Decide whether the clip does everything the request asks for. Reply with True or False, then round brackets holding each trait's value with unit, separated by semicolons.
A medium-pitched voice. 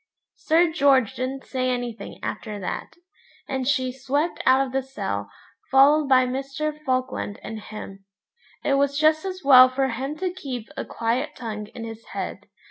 False (265 Hz)